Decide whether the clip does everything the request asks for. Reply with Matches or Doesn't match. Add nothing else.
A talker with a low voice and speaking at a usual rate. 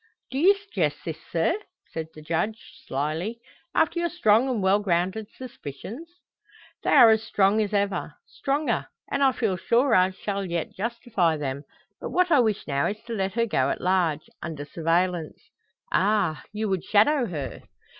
Doesn't match